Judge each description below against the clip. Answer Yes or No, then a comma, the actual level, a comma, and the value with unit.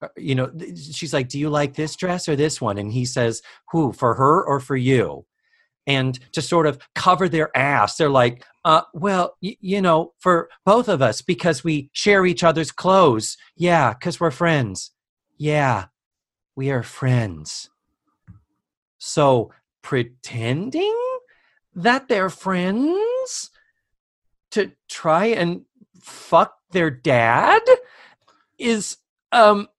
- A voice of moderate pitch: Yes, medium, 165 Hz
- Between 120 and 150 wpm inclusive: Yes, slow, 135 wpm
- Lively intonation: Yes, wide, 6.5 semitones